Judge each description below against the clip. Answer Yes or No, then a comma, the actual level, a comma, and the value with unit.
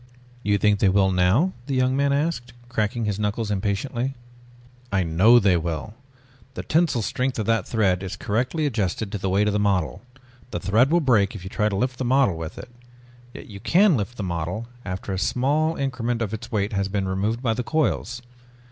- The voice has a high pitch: No, low, 110 Hz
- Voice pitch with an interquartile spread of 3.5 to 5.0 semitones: Yes, average, 4.4 semitones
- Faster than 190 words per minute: Yes, fast, 205 wpm